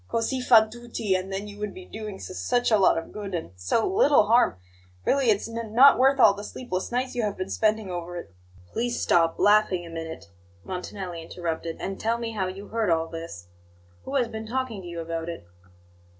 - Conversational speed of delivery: No, fast, 215 wpm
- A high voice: Yes, high, 205 Hz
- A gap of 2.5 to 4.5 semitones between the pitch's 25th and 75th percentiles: No, average, 4.9 semitones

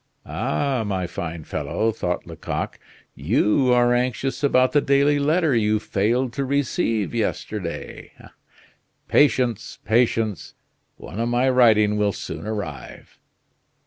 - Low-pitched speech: Yes, low, 115 Hz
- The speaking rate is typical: No, slow, 115 wpm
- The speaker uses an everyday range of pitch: Yes, average, 3.8 semitones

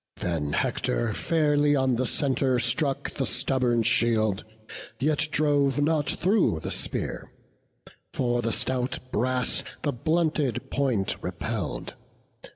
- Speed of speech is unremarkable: No, slow, 115 wpm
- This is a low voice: Yes, low, 130 Hz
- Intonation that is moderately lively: Yes, average, 3.6 semitones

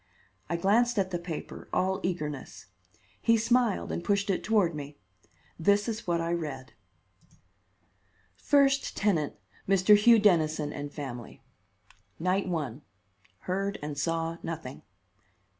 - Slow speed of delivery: Yes, slow, 125 wpm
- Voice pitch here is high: No, medium, 175 Hz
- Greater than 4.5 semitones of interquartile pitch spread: Yes, average, 5.2 semitones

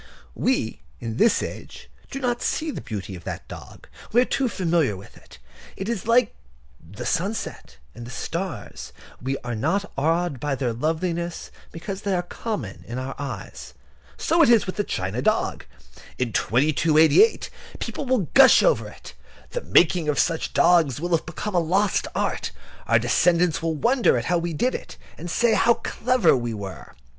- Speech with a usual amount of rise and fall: No, wide, 8.4 semitones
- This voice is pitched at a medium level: Yes, medium, 170 Hz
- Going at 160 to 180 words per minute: Yes, average, 175 wpm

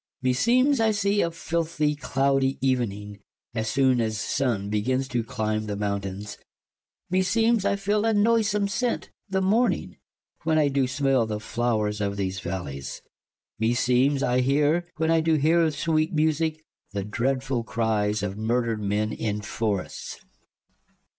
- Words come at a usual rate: Yes, average, 165 wpm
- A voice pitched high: No, low, 130 Hz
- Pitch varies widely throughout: Yes, wide, 7.1 semitones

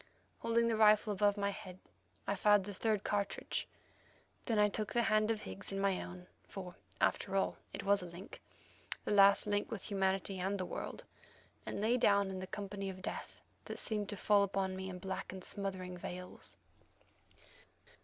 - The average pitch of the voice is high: Yes, high, 200 Hz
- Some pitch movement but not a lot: No, narrow, 1.7 semitones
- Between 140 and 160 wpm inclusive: No, average, 175 wpm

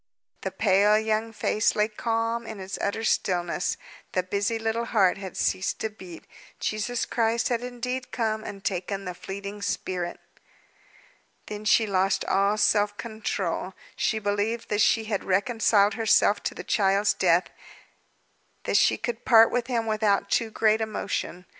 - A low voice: No, high, 210 Hz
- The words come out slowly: No, average, 155 wpm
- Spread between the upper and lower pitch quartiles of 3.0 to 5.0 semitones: No, narrow, 2.4 semitones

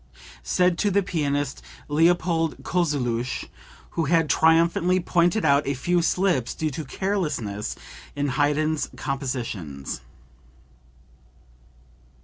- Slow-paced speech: Yes, slow, 100 wpm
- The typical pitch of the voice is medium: Yes, medium, 155 Hz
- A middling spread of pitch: Yes, average, 4.2 semitones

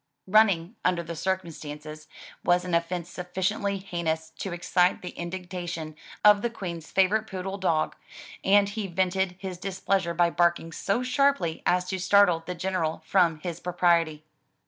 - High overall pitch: No, medium, 180 Hz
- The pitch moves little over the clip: Yes, narrow, 2.3 semitones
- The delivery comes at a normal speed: Yes, average, 145 wpm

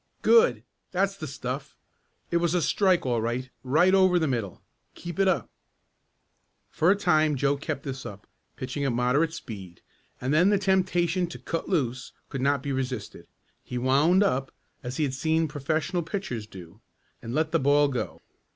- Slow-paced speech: No, average, 175 wpm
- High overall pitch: No, medium, 145 Hz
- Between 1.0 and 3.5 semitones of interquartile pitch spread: No, wide, 5.4 semitones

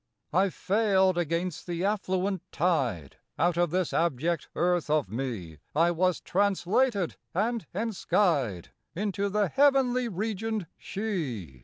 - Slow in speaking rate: Yes, slow, 120 wpm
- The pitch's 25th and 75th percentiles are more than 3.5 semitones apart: Yes, average, 4.1 semitones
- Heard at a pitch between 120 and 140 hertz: No, medium, 180 Hz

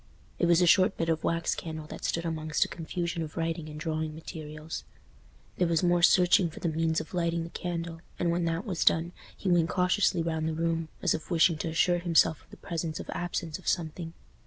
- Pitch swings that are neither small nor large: No, narrow, 1.4 semitones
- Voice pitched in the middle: Yes, medium, 165 Hz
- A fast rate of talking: Yes, fast, 220 wpm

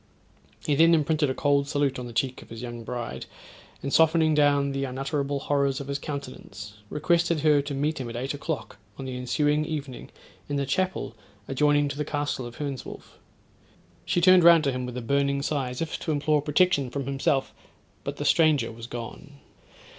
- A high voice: No, medium, 140 Hz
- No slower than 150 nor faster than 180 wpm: No, average, 190 wpm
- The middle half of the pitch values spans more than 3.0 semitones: No, narrow, 2.5 semitones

